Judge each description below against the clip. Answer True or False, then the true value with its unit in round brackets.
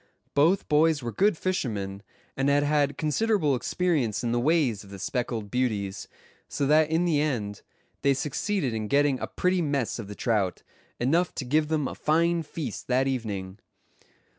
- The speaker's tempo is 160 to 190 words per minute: True (170 wpm)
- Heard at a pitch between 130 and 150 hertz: True (140 Hz)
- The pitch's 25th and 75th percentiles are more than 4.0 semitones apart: True (5.4 semitones)